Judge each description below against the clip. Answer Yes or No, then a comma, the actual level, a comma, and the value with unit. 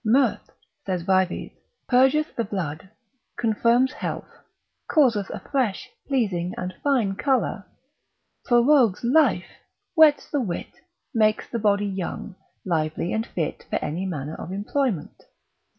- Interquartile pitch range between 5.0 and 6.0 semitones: Yes, wide, 5.5 semitones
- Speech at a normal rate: No, slow, 120 wpm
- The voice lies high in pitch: Yes, high, 215 Hz